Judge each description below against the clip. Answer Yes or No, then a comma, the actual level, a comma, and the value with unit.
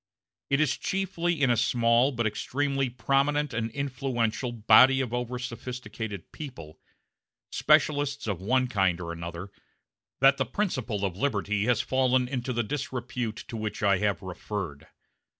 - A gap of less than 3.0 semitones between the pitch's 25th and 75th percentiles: No, average, 4.5 semitones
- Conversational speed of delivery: Yes, average, 145 wpm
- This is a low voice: Yes, low, 120 Hz